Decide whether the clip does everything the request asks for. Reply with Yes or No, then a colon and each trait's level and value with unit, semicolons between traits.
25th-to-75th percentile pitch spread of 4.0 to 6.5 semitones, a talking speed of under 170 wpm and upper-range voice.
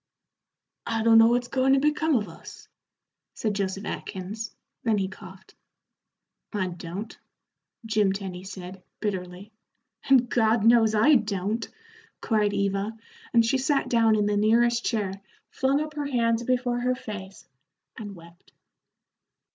No: average, 3.4 semitones; average, 140 wpm; high, 220 Hz